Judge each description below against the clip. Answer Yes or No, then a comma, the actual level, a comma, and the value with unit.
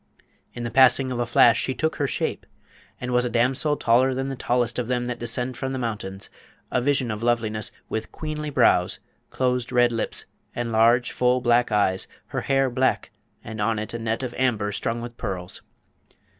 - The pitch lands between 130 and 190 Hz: No, low, 120 Hz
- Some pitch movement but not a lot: No, narrow, 2.1 semitones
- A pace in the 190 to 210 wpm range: Yes, average, 195 wpm